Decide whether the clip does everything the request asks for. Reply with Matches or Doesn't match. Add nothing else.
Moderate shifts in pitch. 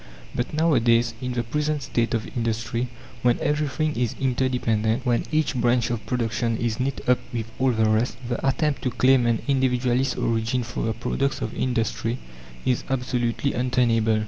Doesn't match